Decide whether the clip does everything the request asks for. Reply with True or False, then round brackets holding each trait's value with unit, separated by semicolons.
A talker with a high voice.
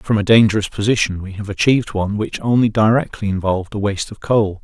False (105 Hz)